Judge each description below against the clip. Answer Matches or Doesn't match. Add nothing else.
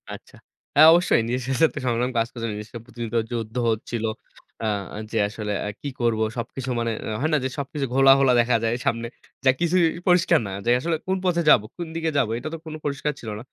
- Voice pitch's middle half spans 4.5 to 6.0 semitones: Matches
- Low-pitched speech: Matches